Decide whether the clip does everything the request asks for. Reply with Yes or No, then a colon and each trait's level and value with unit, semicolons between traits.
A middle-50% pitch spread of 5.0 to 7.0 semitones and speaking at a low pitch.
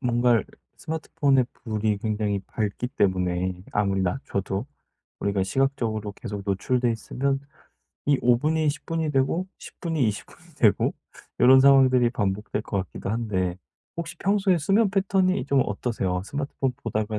Yes: wide, 5.6 semitones; low, 120 Hz